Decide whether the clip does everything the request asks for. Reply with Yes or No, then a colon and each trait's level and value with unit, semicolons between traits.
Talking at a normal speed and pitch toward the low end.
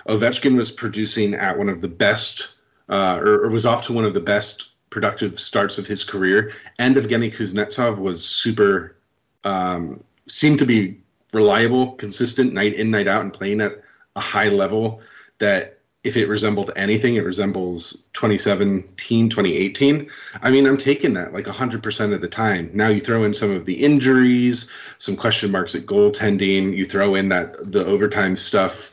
Yes: average, 170 wpm; low, 110 Hz